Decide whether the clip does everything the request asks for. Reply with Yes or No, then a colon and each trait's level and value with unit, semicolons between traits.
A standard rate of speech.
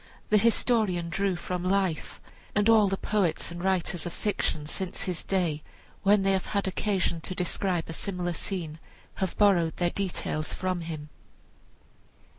Yes: average, 155 wpm